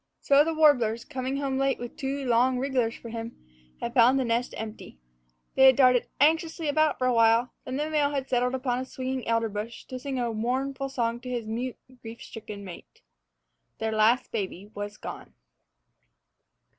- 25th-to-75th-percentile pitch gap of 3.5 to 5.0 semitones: No, average, 2.9 semitones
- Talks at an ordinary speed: Yes, average, 185 wpm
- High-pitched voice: Yes, very high, 250 Hz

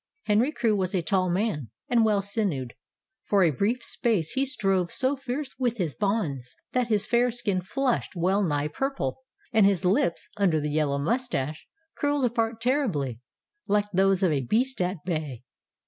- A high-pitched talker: Yes, high, 200 Hz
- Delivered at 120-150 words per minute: No, average, 175 wpm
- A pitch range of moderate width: No, wide, 6.3 semitones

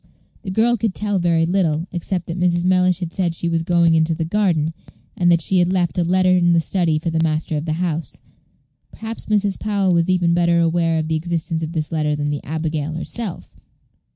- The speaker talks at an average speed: No, fast, 220 wpm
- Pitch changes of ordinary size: No, narrow, 2.2 semitones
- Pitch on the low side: No, medium, 170 Hz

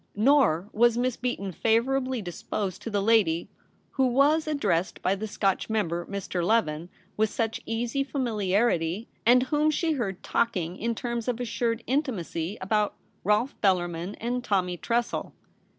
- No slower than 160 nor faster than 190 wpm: No, average, 150 wpm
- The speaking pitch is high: Yes, high, 220 Hz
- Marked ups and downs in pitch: No, average, 4.7 semitones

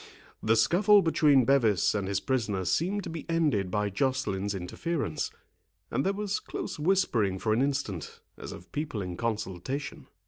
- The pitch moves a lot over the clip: Yes, wide, 7.8 semitones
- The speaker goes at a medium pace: Yes, average, 160 wpm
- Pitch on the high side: No, low, 125 Hz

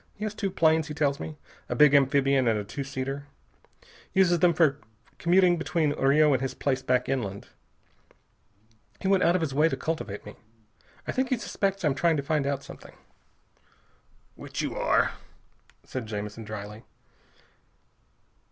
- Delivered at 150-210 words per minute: Yes, average, 160 wpm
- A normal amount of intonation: Yes, average, 4.3 semitones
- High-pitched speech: No, medium, 145 Hz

